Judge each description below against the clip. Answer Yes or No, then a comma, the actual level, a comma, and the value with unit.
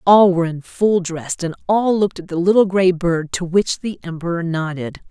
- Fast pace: Yes, fast, 210 wpm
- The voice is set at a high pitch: No, medium, 180 Hz